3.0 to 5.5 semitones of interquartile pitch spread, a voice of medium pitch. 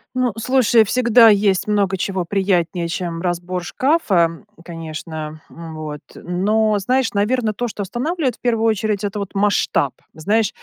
No: average, 4.5 semitones; high, 200 Hz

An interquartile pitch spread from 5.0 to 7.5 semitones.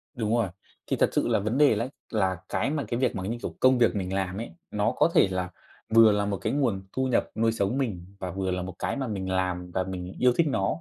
No: average, 4.2 semitones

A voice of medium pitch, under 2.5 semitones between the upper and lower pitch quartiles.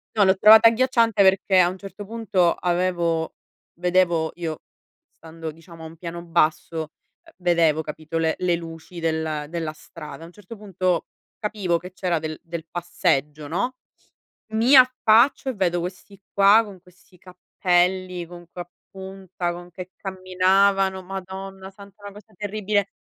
No: medium, 180 Hz; average, 2.8 semitones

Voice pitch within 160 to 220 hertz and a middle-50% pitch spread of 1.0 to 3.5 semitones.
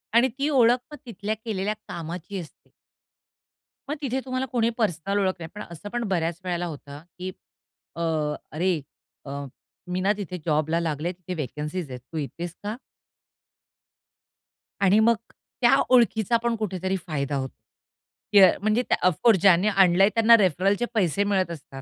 No: medium, 185 Hz; average, 4.6 semitones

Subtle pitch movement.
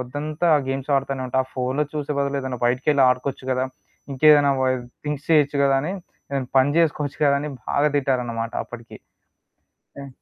Yes: narrow, 2.2 semitones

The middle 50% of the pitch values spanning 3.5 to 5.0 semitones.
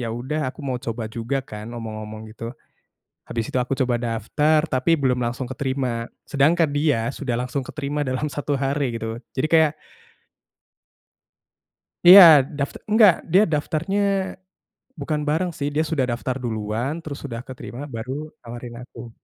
Yes: average, 4.0 semitones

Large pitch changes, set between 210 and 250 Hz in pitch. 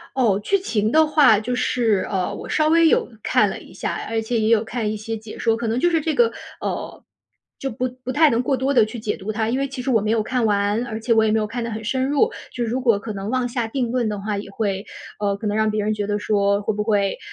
No: average, 3.1 semitones; high, 225 Hz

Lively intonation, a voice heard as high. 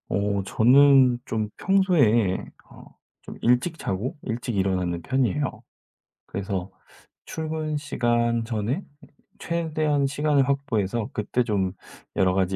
No: wide, 6.0 semitones; low, 120 Hz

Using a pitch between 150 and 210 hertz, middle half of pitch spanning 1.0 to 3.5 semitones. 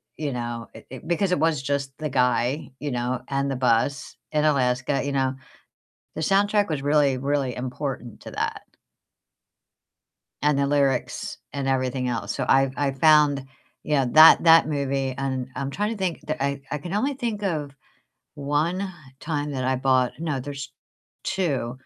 No: medium, 140 Hz; average, 2.9 semitones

